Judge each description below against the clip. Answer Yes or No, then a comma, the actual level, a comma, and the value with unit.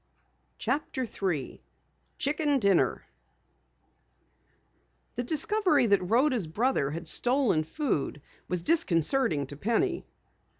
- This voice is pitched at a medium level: No, high, 235 Hz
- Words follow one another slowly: Yes, slow, 90 wpm